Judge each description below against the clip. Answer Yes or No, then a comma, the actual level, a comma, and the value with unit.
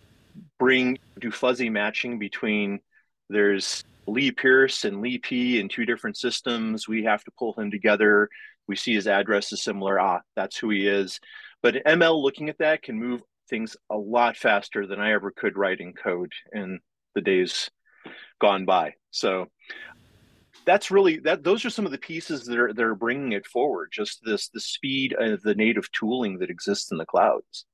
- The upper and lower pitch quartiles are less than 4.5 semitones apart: No, average, 4.8 semitones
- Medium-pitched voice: No, low, 120 Hz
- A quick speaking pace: No, average, 185 wpm